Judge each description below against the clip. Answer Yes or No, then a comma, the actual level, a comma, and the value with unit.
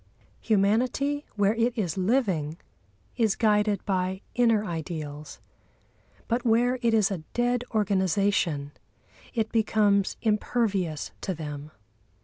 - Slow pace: Yes, slow, 110 wpm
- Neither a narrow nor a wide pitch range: Yes, average, 4.0 semitones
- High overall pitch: Yes, high, 205 Hz